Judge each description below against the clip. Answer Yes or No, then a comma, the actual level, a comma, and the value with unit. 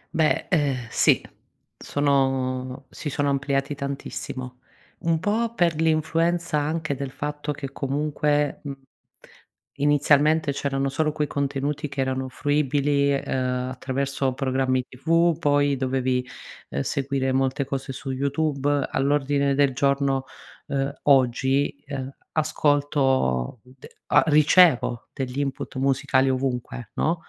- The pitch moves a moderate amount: No, narrow, 1.8 semitones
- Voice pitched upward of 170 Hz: No, medium, 140 Hz